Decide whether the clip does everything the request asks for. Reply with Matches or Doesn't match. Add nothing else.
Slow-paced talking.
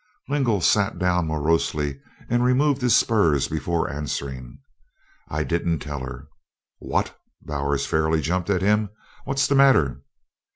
Matches